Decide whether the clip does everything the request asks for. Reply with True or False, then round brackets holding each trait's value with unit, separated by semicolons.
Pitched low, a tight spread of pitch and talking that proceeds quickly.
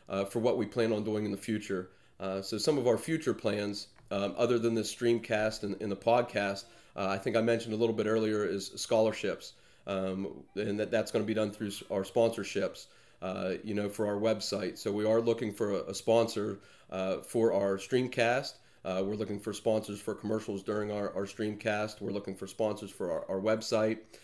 True (105 Hz; 2.2 semitones; 215 wpm)